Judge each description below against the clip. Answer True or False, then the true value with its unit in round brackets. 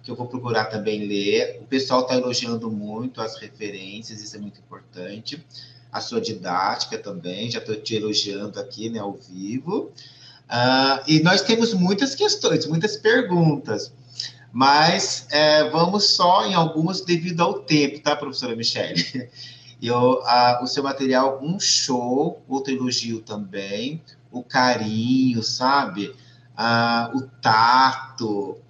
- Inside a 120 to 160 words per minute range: True (135 wpm)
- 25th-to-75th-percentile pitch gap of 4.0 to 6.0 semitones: True (4.4 semitones)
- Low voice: True (125 Hz)